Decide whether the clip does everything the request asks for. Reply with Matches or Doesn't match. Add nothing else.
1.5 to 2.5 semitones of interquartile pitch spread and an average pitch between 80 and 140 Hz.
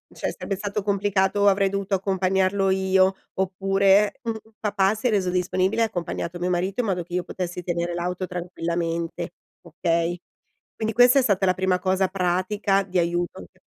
Doesn't match